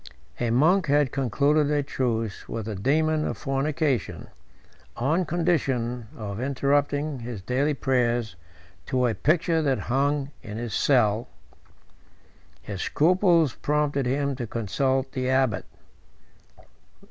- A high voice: No, low, 135 Hz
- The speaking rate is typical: No, slow, 120 wpm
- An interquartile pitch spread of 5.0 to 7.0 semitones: No, average, 3.7 semitones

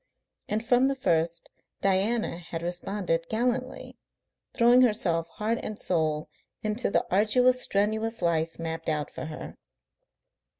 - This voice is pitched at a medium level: No, high, 200 Hz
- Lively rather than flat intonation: Yes, wide, 5.8 semitones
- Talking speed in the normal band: No, slow, 125 wpm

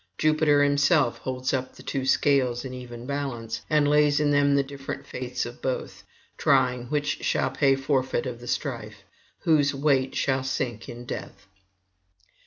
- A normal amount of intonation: No, narrow, 2.3 semitones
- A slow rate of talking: No, average, 160 wpm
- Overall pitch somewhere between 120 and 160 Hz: Yes, low, 135 Hz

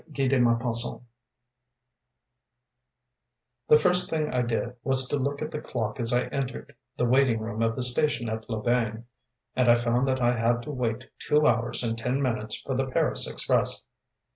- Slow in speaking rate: No, average, 170 wpm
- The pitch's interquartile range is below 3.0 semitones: Yes, narrow, 2.4 semitones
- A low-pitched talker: Yes, low, 120 Hz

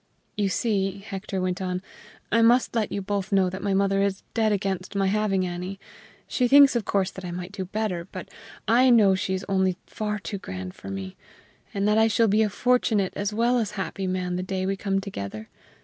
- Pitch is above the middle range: Yes, high, 195 Hz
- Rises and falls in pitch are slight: Yes, narrow, 2.3 semitones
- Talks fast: Yes, fast, 215 wpm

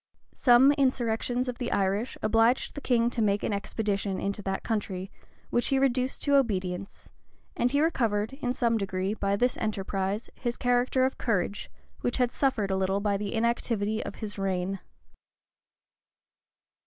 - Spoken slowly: No, average, 160 wpm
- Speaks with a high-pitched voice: Yes, high, 220 Hz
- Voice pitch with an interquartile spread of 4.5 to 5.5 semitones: No, average, 3.8 semitones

